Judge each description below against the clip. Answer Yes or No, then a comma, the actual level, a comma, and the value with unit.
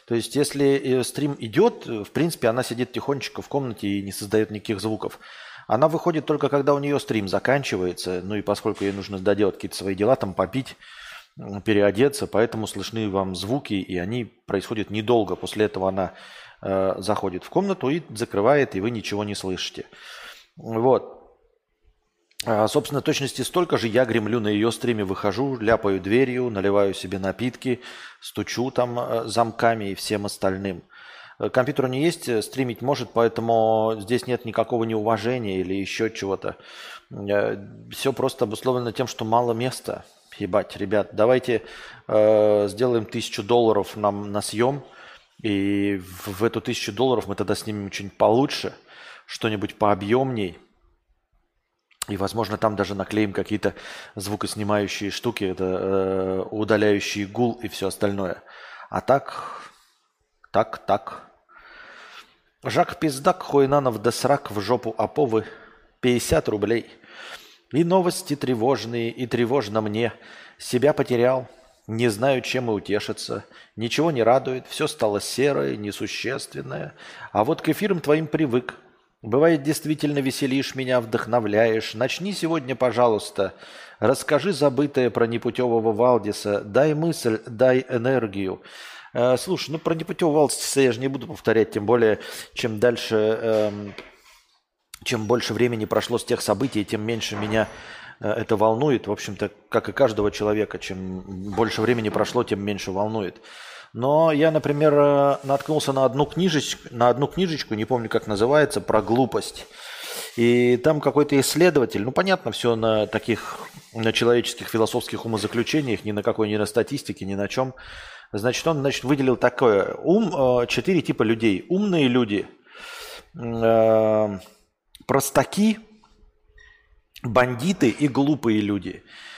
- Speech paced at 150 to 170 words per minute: No, average, 135 wpm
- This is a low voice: Yes, low, 115 Hz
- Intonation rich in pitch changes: No, average, 4.7 semitones